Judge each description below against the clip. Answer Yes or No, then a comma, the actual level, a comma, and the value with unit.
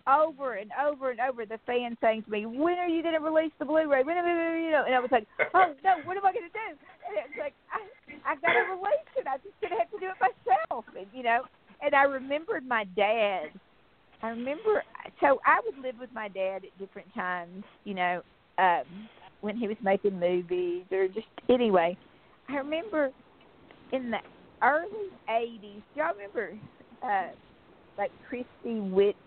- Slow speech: No, average, 195 wpm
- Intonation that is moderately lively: No, wide, 7.4 semitones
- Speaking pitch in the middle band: No, very high, 265 Hz